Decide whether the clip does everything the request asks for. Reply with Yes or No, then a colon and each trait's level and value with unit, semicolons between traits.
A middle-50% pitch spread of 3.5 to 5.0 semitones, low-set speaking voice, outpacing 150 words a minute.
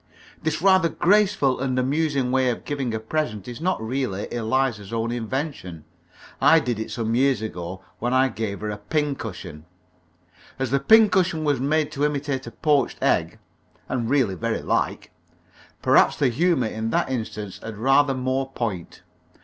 Yes: average, 4.6 semitones; low, 130 Hz; average, 160 wpm